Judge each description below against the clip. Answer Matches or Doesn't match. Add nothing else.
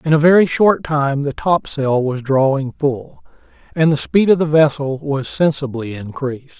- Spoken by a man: Matches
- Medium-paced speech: Matches